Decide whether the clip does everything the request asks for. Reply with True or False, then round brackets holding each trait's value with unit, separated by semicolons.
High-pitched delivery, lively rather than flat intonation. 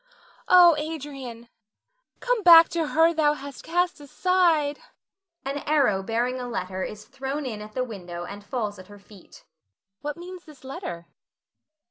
True (275 Hz; 7.2 semitones)